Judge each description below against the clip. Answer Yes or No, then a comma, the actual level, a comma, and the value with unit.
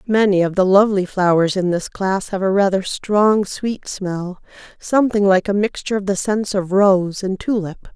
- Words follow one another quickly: No, average, 190 wpm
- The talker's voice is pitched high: Yes, high, 195 Hz